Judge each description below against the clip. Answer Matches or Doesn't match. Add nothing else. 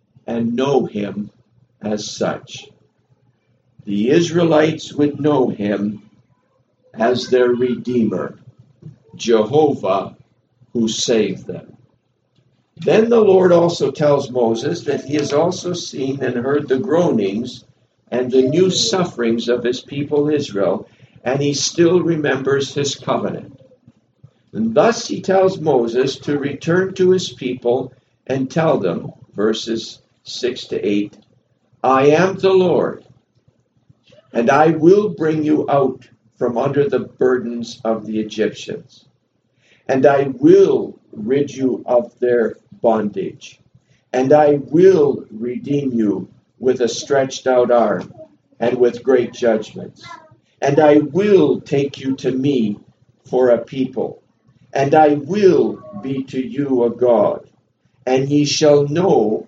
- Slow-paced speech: Matches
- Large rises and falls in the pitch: Doesn't match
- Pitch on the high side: Doesn't match